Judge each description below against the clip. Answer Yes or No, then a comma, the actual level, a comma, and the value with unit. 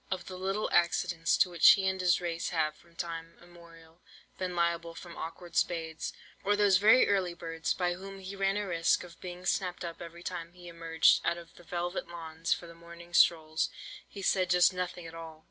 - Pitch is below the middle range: No, medium, 175 Hz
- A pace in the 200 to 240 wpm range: Yes, fast, 205 wpm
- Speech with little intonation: Yes, narrow, 1.6 semitones